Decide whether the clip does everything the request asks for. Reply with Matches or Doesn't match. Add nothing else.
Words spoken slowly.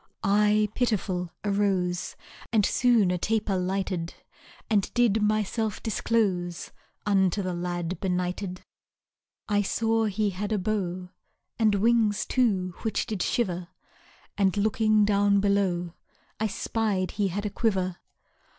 Matches